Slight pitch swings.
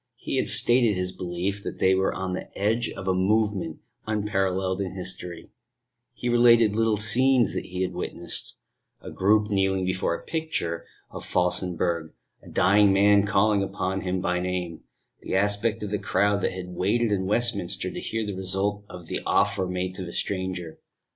Yes: narrow, 2.3 semitones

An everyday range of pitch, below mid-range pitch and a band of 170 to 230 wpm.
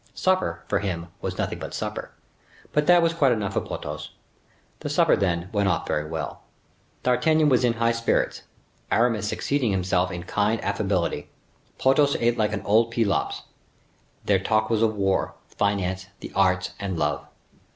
No: average, 4.0 semitones; low, 105 Hz; average, 160 wpm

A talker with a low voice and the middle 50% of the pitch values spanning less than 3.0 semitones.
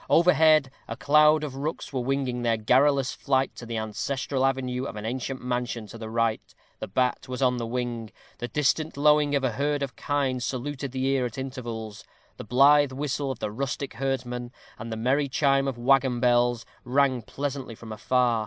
Yes: low, 130 Hz; narrow, 2.5 semitones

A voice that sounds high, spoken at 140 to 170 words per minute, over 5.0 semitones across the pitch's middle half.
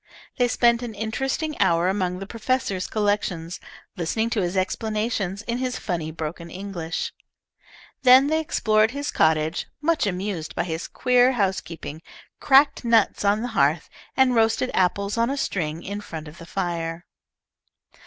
Yes: high, 205 Hz; average, 150 wpm; wide, 5.6 semitones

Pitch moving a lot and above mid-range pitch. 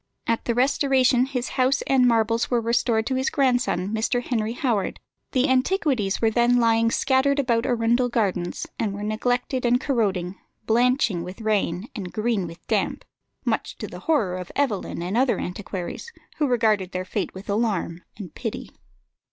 No: average, 3.9 semitones; high, 230 Hz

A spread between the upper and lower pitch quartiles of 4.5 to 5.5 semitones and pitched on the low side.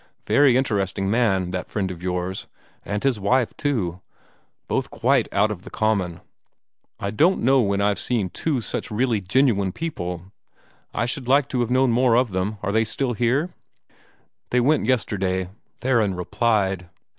Yes: average, 4.9 semitones; low, 110 Hz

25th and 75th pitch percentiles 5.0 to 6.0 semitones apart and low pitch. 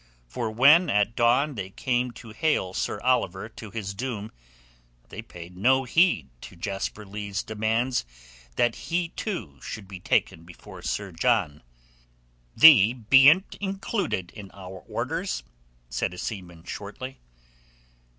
Yes: average, 5.3 semitones; low, 110 Hz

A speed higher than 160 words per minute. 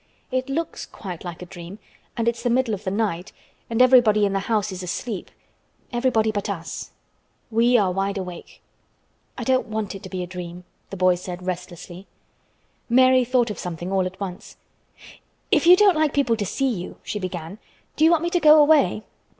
Yes: average, 190 wpm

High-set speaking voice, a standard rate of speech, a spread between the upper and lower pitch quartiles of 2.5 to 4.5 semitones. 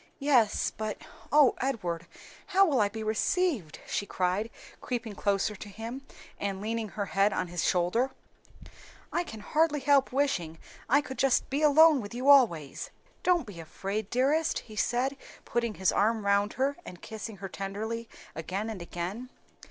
No: high, 220 Hz; average, 160 wpm; wide, 5.4 semitones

